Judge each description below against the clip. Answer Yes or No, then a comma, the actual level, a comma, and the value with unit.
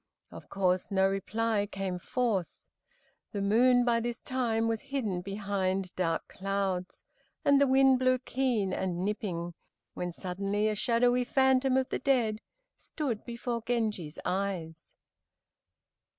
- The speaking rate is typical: No, slow, 130 wpm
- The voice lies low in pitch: No, high, 215 Hz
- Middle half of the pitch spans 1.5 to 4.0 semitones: No, average, 4.5 semitones